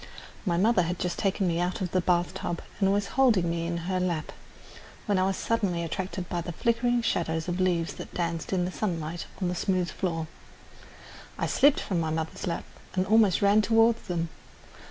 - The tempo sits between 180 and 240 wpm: Yes, average, 195 wpm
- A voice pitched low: No, medium, 180 Hz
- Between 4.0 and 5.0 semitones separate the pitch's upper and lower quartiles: No, average, 2.8 semitones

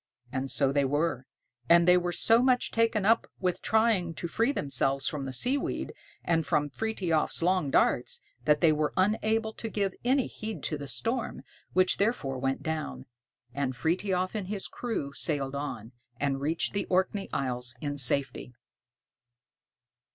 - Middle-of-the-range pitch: Yes, medium, 165 Hz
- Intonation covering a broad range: Yes, wide, 7.0 semitones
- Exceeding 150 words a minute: Yes, average, 160 wpm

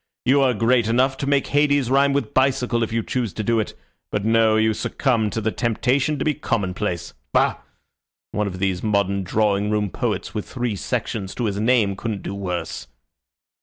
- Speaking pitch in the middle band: No, low, 110 Hz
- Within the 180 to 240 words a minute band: Yes, average, 190 wpm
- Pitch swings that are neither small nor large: Yes, average, 4.0 semitones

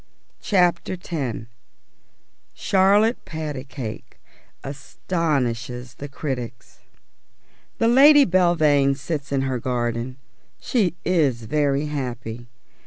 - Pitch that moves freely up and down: Yes, wide, 5.7 semitones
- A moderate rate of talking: No, slow, 85 wpm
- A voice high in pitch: No, medium, 140 Hz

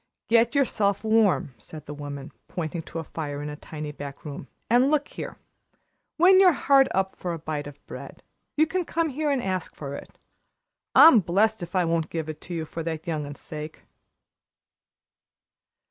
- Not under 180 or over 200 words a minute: Yes, average, 185 wpm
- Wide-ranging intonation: Yes, wide, 7.7 semitones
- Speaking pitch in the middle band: Yes, medium, 170 Hz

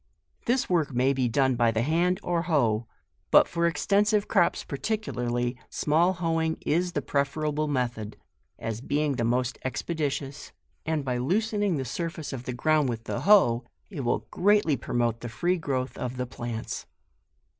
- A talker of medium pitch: Yes, medium, 145 Hz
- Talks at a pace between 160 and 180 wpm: Yes, average, 170 wpm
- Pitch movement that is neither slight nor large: No, wide, 5.7 semitones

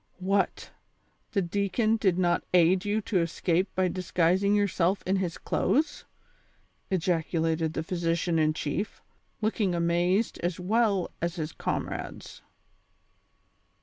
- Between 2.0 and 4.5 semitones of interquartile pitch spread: Yes, average, 2.8 semitones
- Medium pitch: Yes, medium, 180 Hz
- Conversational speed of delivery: No, slow, 130 wpm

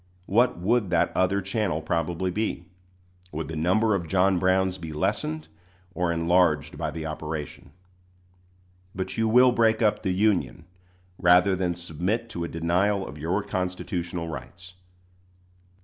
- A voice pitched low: Yes, very low, 90 Hz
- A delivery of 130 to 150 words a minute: Yes, average, 140 wpm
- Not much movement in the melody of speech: No, average, 3.4 semitones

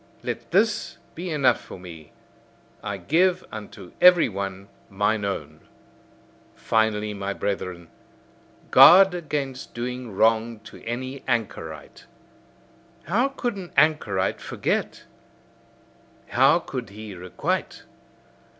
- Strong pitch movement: Yes, wide, 7.3 semitones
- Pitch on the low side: Yes, low, 110 Hz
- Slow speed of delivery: Yes, slow, 105 wpm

